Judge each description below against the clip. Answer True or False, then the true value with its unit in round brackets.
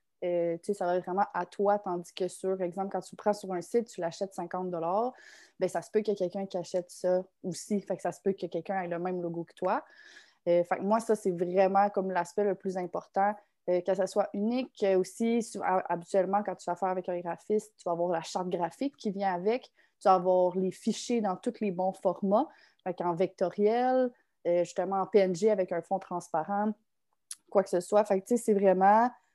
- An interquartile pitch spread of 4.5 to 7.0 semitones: False (2.4 semitones)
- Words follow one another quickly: True (225 wpm)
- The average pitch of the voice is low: False (190 Hz)